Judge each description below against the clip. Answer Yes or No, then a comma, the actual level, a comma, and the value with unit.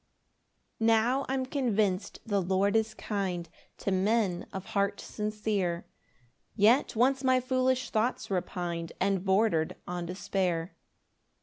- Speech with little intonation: No, average, 3.7 semitones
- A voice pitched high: Yes, high, 205 Hz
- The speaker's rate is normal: No, slow, 120 wpm